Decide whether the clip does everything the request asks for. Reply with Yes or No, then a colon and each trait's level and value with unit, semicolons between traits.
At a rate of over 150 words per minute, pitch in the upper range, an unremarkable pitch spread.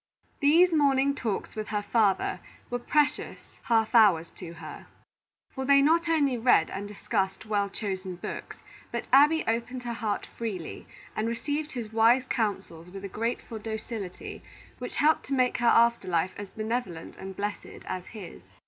Yes: average, 160 wpm; high, 225 Hz; average, 4.9 semitones